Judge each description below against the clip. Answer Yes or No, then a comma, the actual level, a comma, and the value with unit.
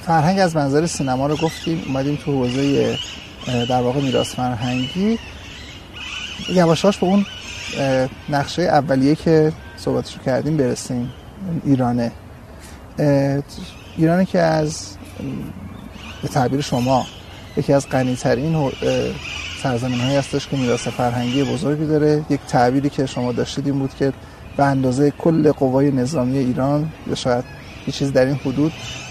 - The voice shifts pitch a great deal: No, average, 3.2 semitones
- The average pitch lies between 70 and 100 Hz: No, low, 135 Hz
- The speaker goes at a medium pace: Yes, average, 130 wpm